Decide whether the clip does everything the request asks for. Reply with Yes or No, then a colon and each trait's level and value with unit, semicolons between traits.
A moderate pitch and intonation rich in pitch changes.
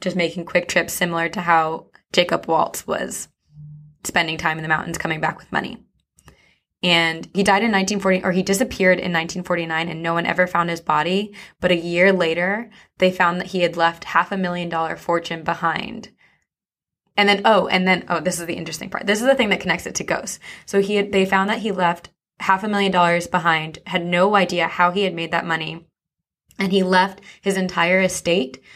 No: medium, 175 Hz; narrow, 2.4 semitones